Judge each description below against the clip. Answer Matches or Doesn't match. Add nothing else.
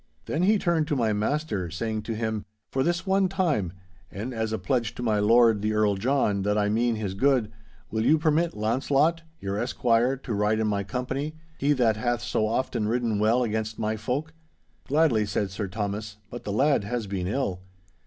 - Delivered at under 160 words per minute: Doesn't match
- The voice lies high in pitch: Doesn't match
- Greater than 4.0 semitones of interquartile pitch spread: Matches